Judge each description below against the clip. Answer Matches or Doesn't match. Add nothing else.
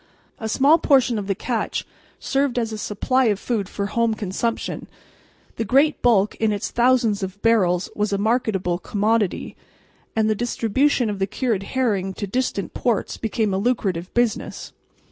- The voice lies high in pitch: Matches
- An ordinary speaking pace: Matches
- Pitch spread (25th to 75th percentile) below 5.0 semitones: Matches